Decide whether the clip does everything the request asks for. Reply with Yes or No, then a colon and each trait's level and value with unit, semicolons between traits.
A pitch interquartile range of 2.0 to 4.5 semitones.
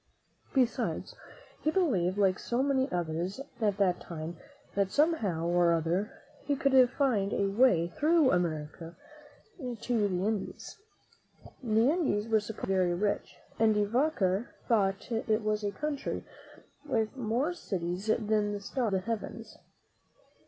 No: average, 5.3 semitones